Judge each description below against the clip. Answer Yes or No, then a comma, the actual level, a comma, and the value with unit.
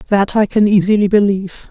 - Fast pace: No, average, 175 wpm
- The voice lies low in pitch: No, high, 200 Hz